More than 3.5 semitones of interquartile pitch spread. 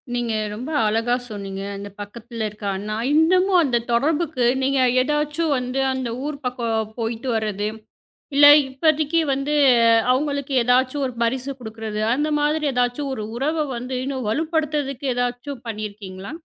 Yes: average, 4.6 semitones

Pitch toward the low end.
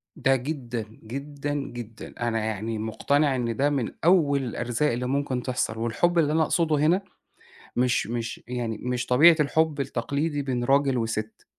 Yes: low, 130 Hz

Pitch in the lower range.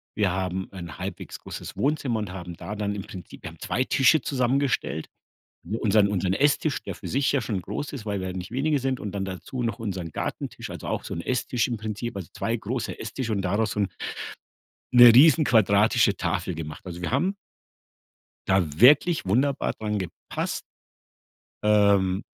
Yes: low, 105 Hz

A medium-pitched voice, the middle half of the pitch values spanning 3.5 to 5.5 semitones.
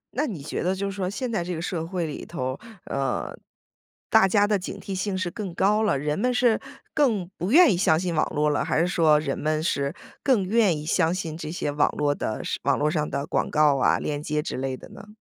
Yes: medium, 170 Hz; average, 4.8 semitones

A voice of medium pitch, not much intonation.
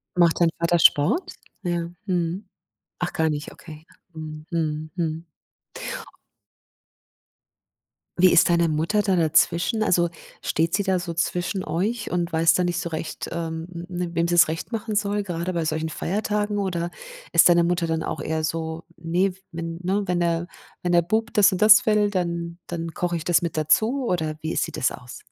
Yes: medium, 170 Hz; narrow, 2.2 semitones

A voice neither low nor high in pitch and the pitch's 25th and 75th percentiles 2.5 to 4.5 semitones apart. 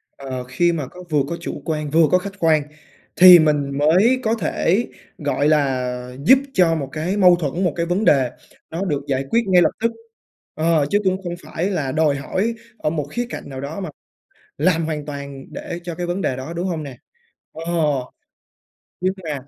Yes: medium, 160 Hz; average, 4.2 semitones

